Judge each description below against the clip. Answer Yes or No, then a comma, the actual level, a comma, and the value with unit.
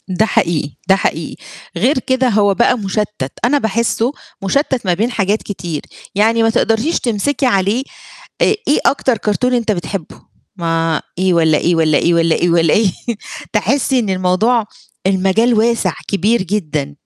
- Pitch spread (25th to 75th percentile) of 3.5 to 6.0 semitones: Yes, average, 5.1 semitones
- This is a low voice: No, high, 205 Hz